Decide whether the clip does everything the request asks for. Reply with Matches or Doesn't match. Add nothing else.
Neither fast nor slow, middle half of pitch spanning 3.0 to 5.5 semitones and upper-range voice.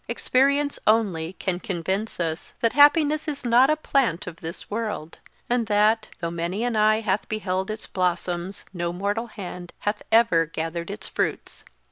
Matches